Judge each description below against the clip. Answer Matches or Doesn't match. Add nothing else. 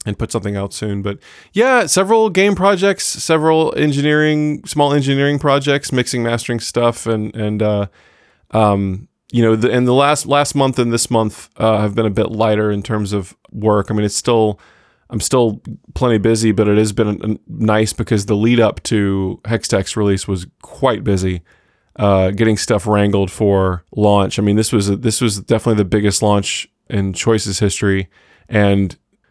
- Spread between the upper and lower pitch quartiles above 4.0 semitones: Doesn't match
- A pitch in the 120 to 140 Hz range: Doesn't match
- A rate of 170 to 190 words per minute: Matches